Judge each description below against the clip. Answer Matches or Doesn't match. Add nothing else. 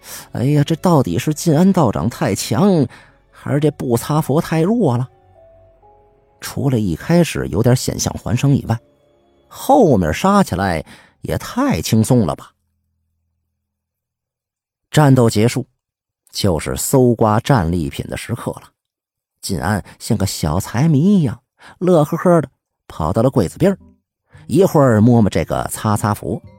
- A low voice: Matches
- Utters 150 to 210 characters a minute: Matches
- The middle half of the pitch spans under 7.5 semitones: Matches